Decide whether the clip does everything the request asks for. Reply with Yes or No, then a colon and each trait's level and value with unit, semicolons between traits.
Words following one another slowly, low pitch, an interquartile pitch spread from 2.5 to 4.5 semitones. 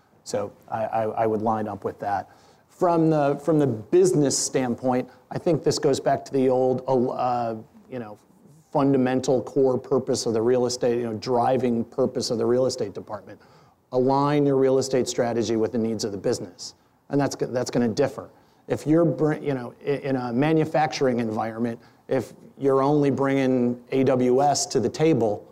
No: average, 175 wpm; low, 130 Hz; average, 2.8 semitones